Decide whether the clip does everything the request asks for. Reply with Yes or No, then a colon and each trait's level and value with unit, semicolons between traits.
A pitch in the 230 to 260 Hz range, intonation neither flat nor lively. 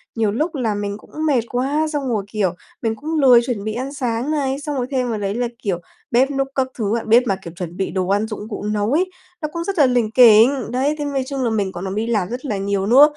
Yes: high, 235 Hz; average, 4.7 semitones